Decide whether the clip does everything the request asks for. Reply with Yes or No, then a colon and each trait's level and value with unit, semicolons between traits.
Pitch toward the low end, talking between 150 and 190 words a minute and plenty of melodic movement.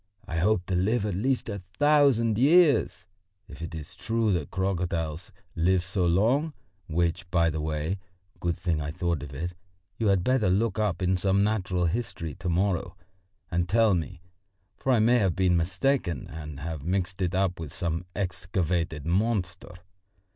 No: very low, 90 Hz; average, 170 wpm; average, 3.8 semitones